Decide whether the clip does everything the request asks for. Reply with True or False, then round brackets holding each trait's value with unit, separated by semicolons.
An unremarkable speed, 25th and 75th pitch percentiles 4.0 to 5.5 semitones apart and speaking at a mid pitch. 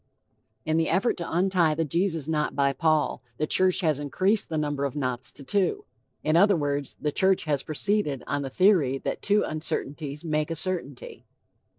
True (185 wpm; 4.4 semitones; 155 Hz)